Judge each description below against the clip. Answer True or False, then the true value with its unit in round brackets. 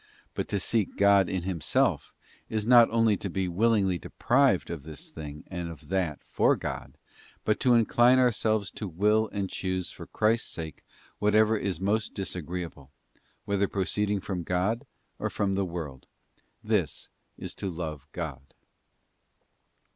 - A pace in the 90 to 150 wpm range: True (145 wpm)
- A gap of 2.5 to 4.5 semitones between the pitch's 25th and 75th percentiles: True (4.0 semitones)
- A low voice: True (95 Hz)